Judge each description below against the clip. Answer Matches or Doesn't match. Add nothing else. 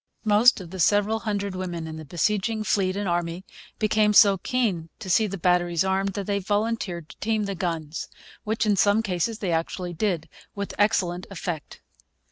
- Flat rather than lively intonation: Doesn't match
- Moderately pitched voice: Doesn't match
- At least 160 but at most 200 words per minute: Matches